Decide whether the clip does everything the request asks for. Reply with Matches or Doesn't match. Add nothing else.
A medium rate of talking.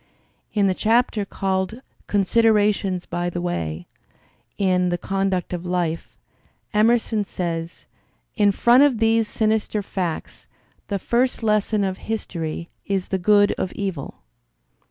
Doesn't match